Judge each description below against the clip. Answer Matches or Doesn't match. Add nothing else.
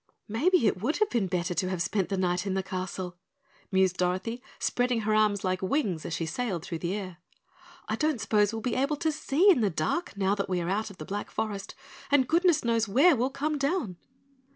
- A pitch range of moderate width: Doesn't match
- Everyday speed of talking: Doesn't match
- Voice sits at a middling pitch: Doesn't match